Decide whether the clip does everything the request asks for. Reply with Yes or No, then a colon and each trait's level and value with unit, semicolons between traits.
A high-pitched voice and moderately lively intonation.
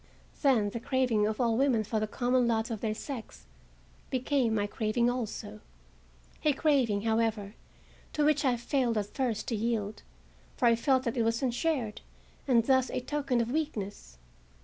Yes: high, 235 Hz; average, 3.1 semitones